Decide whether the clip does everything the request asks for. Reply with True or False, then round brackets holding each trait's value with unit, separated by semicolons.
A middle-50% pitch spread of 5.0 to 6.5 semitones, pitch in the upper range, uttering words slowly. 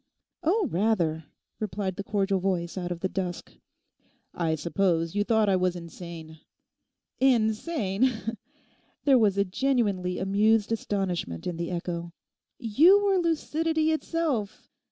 True (5.3 semitones; 200 Hz; 125 wpm)